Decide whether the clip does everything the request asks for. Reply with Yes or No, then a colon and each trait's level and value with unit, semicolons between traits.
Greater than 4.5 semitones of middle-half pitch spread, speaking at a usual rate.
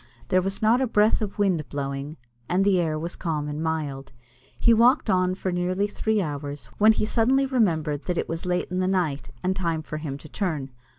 No: average, 5.0 semitones; fast, 215 wpm